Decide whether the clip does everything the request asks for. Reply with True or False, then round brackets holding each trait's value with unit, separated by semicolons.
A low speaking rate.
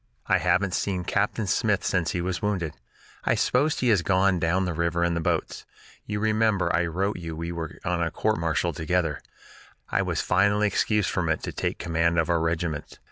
False (200 wpm)